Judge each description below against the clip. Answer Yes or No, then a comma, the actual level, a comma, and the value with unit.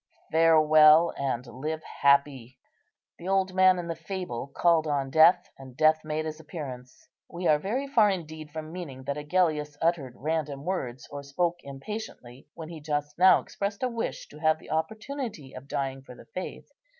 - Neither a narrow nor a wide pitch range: Yes, average, 4.0 semitones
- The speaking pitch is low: No, medium, 155 Hz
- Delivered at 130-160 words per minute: No, average, 175 wpm